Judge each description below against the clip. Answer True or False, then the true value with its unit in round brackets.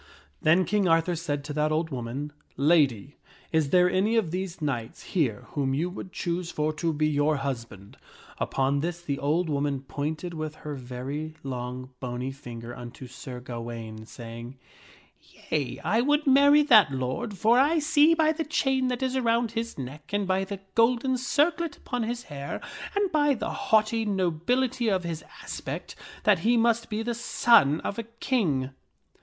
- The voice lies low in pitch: False (165 Hz)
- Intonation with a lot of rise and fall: True (8.9 semitones)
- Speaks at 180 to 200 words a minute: True (185 wpm)